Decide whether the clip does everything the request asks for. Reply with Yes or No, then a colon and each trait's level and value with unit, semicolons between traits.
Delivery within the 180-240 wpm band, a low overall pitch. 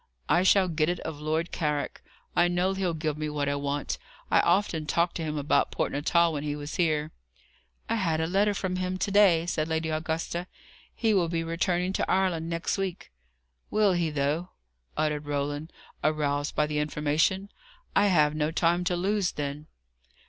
No: average, 185 wpm; medium, 165 Hz